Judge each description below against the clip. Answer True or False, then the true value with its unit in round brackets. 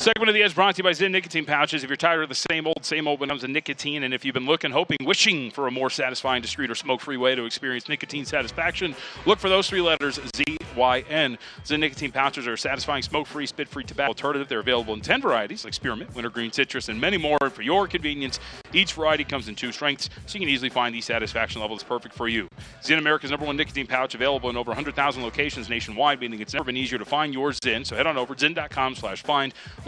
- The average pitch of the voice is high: False (140 Hz)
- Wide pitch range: False (3.2 semitones)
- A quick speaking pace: True (250 wpm)